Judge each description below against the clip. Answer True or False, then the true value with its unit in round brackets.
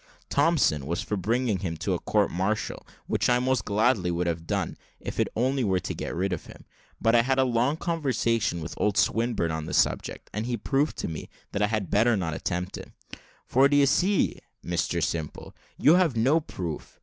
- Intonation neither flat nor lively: False (6.8 semitones)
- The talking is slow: False (205 wpm)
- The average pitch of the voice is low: True (110 Hz)